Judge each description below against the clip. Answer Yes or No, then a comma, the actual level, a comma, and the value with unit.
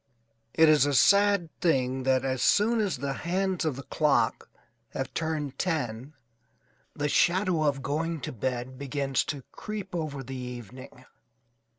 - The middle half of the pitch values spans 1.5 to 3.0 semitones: No, average, 4.4 semitones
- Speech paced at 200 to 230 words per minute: No, average, 150 wpm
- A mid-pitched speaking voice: Yes, medium, 145 Hz